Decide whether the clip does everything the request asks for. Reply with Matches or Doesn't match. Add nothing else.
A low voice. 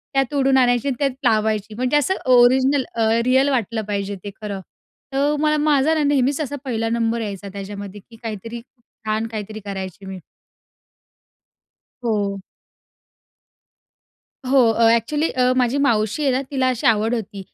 Doesn't match